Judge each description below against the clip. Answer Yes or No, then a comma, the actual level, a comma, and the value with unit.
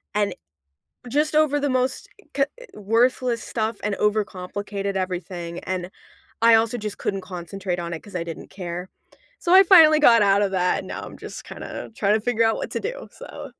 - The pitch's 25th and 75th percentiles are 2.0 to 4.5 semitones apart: No, average, 4.9 semitones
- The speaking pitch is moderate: No, high, 210 Hz